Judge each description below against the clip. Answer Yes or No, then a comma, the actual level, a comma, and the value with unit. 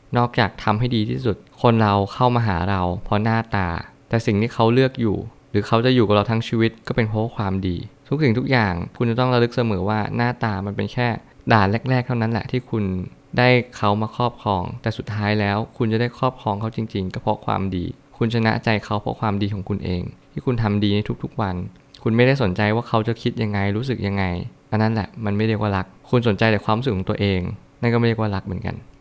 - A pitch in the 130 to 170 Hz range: No, low, 110 Hz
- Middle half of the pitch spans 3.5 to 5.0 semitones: No, average, 3.0 semitones